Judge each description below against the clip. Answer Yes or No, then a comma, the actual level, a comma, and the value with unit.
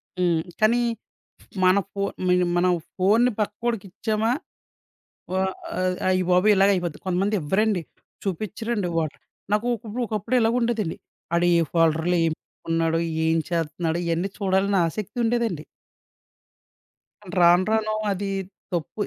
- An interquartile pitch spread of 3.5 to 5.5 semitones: Yes, average, 3.8 semitones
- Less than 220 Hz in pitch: Yes, high, 190 Hz